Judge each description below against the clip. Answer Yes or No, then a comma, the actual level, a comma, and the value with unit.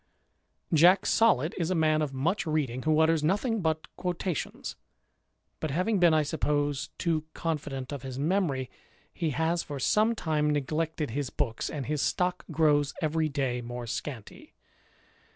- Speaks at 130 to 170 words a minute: Yes, average, 150 wpm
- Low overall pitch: No, medium, 155 Hz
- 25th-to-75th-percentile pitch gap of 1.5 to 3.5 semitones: Yes, average, 2.9 semitones